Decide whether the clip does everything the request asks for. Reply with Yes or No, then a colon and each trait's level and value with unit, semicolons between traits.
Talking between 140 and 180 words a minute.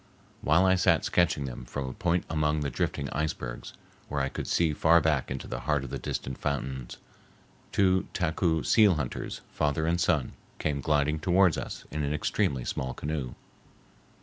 Yes: average, 175 wpm